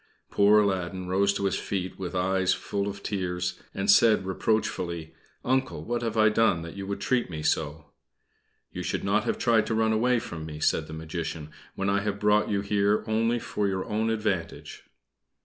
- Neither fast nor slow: Yes, average, 190 wpm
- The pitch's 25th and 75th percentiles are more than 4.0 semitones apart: No, average, 3.3 semitones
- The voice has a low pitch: Yes, low, 100 Hz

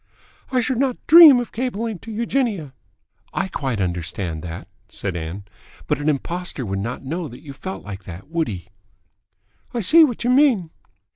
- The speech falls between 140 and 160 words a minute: No, average, 170 wpm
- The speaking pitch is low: No, medium, 165 Hz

